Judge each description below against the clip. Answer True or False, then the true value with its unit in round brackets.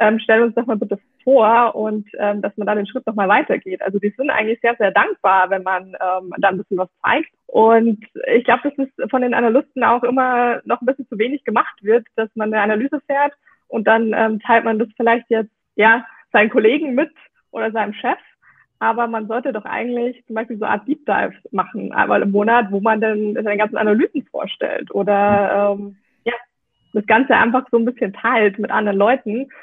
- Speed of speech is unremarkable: False (215 wpm)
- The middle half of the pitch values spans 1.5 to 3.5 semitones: True (2.9 semitones)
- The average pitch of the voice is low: False (225 Hz)